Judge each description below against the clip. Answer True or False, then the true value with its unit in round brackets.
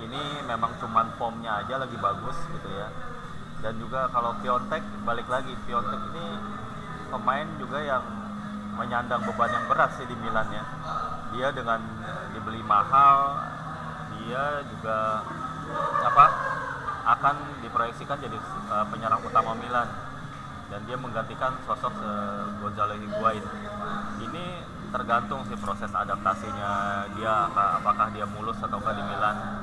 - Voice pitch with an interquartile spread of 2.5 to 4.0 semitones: True (2.8 semitones)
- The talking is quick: False (120 wpm)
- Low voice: True (105 Hz)